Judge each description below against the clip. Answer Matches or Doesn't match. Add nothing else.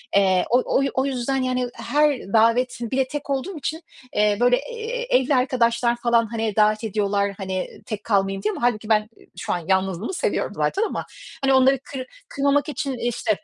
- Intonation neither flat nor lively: Matches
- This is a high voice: Matches